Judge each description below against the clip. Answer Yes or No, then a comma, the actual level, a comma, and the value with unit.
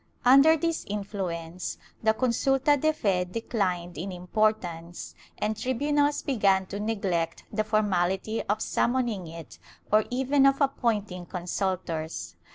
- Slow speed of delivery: Yes, slow, 120 wpm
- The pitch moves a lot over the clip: Yes, wide, 5.8 semitones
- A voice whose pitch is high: Yes, high, 210 Hz